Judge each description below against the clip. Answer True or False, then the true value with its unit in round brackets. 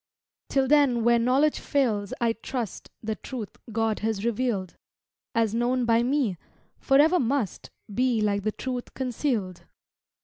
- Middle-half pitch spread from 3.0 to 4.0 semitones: True (3.3 semitones)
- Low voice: False (235 Hz)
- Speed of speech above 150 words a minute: False (135 wpm)